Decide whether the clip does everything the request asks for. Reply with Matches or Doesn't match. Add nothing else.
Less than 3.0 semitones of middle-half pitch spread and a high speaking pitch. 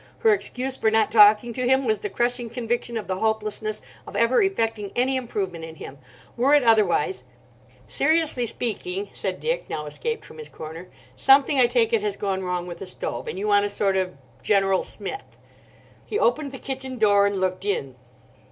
Doesn't match